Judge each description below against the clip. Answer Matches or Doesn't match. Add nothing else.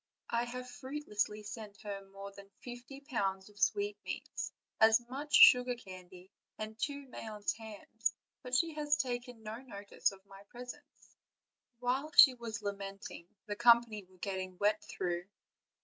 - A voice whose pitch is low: Doesn't match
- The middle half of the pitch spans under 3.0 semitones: Doesn't match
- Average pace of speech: Matches